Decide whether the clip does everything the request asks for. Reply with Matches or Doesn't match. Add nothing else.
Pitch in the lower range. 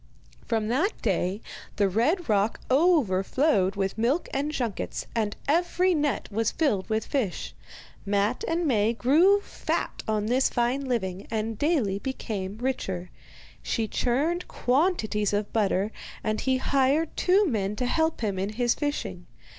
Doesn't match